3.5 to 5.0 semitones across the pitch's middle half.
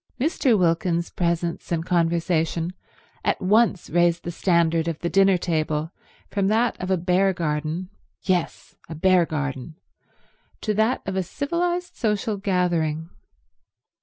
No: average, 3.0 semitones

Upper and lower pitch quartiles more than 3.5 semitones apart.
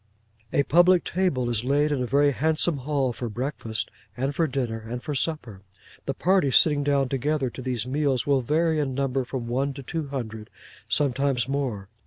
No: average, 3.0 semitones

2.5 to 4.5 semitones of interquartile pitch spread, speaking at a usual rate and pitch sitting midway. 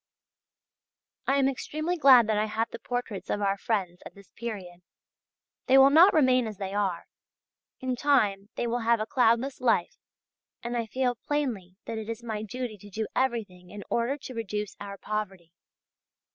No: average, 3.9 semitones; average, 175 wpm; high, 225 Hz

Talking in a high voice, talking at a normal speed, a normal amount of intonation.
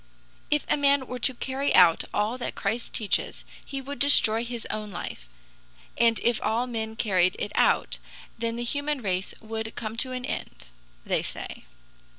Yes: high, 230 Hz; average, 170 wpm; average, 3.2 semitones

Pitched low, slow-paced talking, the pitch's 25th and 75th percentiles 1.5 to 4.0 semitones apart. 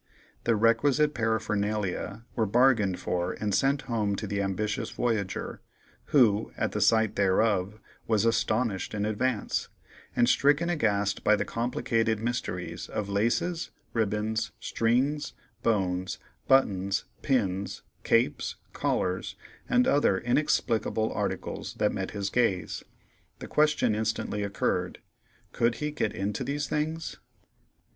Yes: low, 110 Hz; slow, 120 wpm; average, 3.6 semitones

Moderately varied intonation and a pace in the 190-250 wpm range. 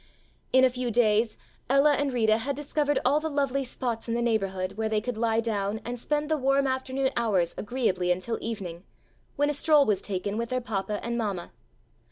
Yes: average, 4.4 semitones; average, 200 wpm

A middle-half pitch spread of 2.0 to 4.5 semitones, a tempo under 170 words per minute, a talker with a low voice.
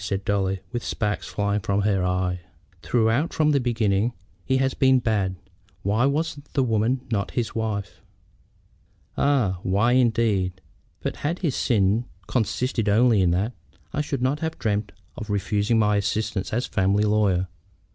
Yes: average, 3.8 semitones; average, 155 wpm; low, 110 Hz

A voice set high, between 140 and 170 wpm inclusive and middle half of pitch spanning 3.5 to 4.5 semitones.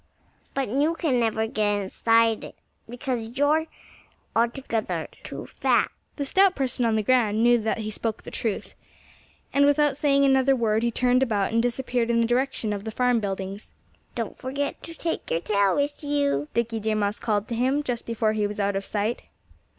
No: high, 235 Hz; average, 190 wpm; average, 3.8 semitones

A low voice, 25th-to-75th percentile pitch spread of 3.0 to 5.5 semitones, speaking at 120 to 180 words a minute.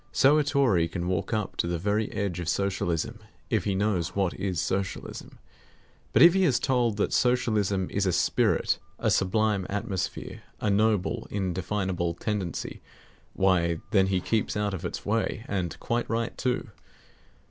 Yes: low, 100 Hz; average, 3.3 semitones; average, 160 wpm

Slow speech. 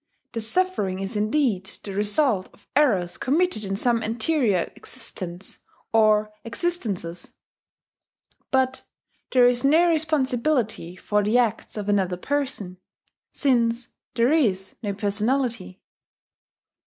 Yes: slow, 110 wpm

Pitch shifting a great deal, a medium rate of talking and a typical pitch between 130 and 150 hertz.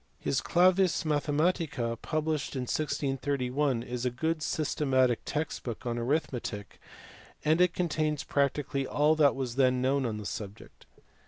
No: average, 3.6 semitones; average, 145 wpm; medium, 140 Hz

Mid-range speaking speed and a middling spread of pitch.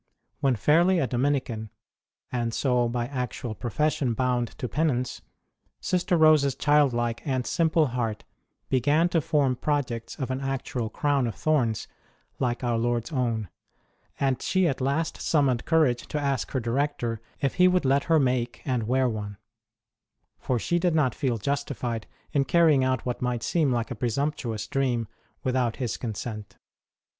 Yes: average, 165 wpm; average, 3.4 semitones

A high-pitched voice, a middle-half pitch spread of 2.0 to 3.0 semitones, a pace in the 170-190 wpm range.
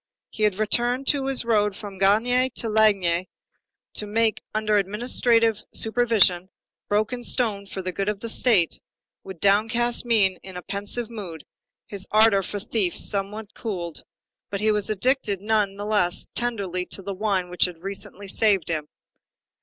No: high, 210 Hz; average, 2.7 semitones; average, 155 wpm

